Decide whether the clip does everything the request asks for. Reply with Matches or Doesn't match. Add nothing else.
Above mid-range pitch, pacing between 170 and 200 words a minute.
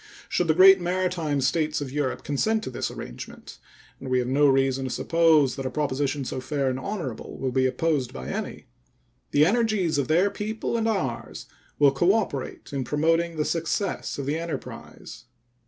Doesn't match